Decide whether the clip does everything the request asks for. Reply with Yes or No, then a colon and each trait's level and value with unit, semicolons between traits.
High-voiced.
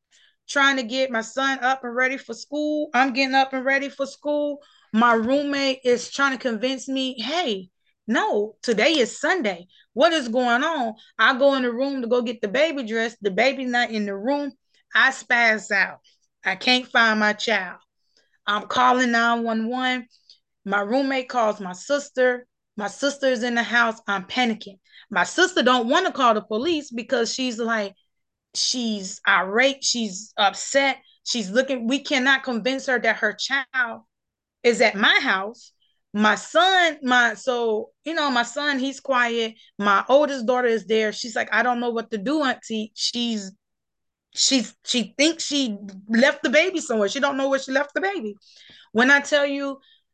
Yes: very high, 250 Hz